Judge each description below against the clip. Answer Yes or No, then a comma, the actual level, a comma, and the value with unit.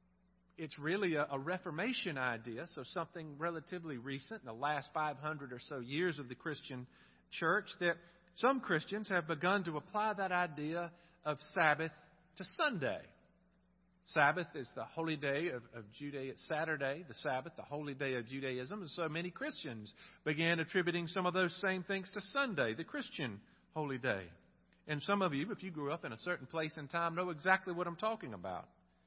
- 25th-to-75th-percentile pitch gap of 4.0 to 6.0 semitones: Yes, average, 4.3 semitones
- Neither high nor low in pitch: Yes, medium, 165 Hz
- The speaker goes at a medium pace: Yes, average, 180 wpm